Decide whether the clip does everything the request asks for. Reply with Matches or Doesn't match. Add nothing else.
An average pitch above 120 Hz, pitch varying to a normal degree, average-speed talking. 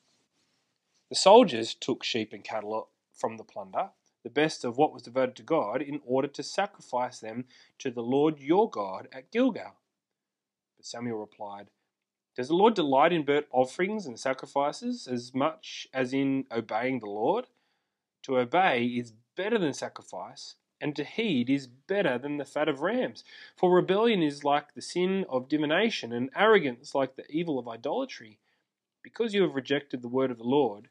Matches